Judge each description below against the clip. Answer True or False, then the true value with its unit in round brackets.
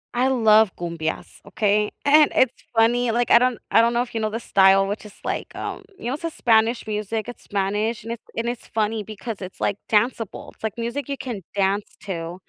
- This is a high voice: True (220 Hz)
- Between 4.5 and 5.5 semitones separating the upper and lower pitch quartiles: False (2.8 semitones)